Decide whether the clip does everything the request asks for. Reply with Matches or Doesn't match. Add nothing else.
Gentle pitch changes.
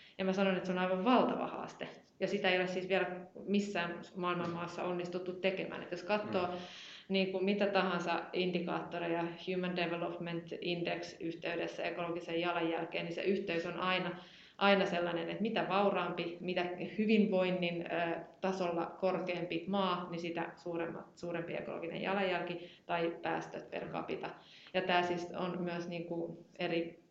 Matches